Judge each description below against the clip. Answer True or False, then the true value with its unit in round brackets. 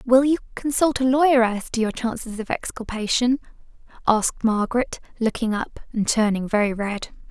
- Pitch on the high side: True (235 Hz)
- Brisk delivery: False (155 wpm)